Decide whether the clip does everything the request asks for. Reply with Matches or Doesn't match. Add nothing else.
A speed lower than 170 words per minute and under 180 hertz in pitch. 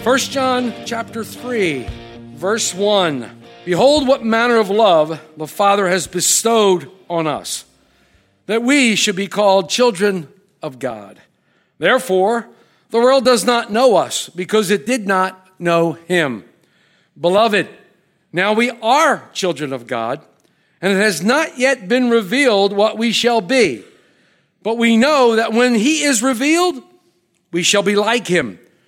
Doesn't match